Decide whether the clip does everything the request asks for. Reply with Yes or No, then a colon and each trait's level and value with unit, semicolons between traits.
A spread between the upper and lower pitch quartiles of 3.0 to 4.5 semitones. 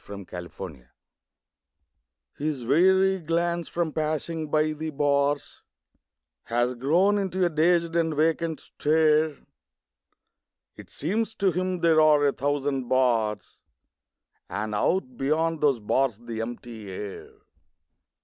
No: average, 5.3 semitones